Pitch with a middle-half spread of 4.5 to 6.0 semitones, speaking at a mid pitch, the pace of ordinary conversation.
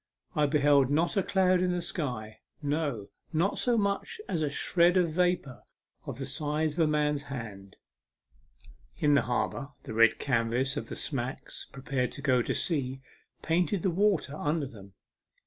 Yes: average, 4.9 semitones; medium, 145 Hz; average, 165 wpm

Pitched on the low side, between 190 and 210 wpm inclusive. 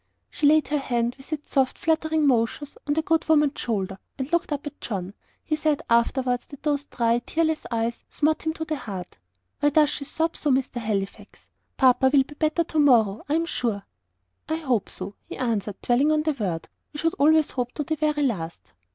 No: very high, 280 Hz; fast, 205 wpm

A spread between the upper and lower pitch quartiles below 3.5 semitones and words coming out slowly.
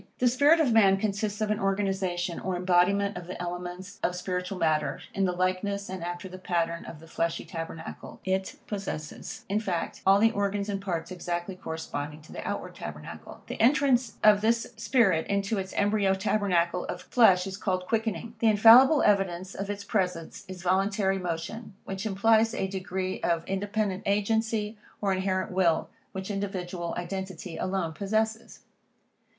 No: narrow, 2.6 semitones; average, 165 wpm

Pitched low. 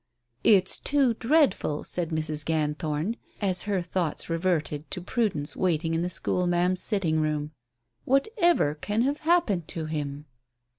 No: medium, 175 Hz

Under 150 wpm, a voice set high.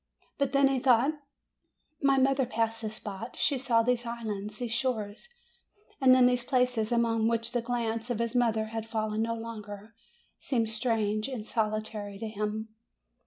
No: average, 165 wpm; high, 230 Hz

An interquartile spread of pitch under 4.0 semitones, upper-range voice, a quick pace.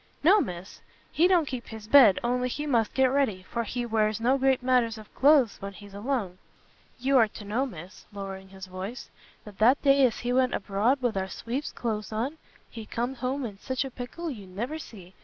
No: average, 4.4 semitones; high, 235 Hz; fast, 210 wpm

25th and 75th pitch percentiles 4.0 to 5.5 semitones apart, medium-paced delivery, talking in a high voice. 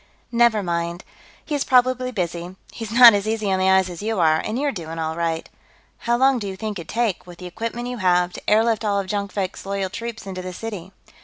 No: average, 4.4 semitones; fast, 225 wpm; high, 200 Hz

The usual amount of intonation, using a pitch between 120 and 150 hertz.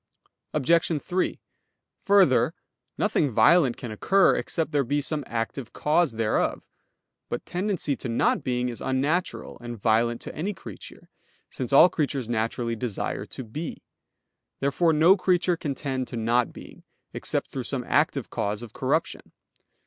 No: wide, 5.7 semitones; low, 135 Hz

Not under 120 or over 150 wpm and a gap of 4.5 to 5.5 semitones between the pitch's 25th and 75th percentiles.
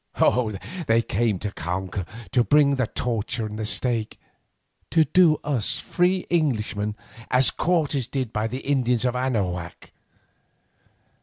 Yes: average, 140 wpm; average, 4.8 semitones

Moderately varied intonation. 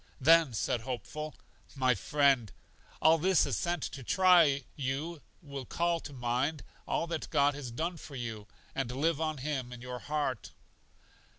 Yes: average, 4.1 semitones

